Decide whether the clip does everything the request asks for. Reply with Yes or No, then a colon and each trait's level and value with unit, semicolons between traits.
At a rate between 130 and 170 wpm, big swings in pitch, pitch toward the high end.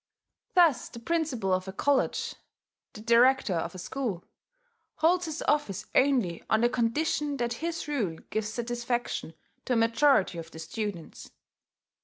Yes: average, 145 wpm; wide, 6.2 semitones; high, 235 Hz